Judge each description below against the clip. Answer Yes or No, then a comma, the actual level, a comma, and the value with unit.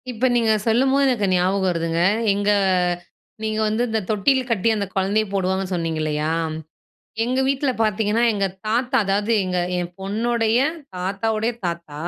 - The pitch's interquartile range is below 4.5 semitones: Yes, average, 3.7 semitones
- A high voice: Yes, high, 210 Hz